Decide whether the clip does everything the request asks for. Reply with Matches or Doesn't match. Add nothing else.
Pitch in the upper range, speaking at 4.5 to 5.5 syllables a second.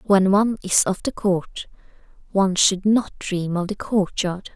Doesn't match